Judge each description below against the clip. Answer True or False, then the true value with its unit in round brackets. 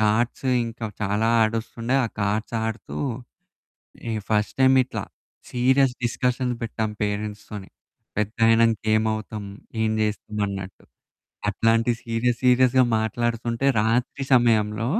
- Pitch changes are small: True (2.2 semitones)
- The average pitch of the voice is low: True (115 Hz)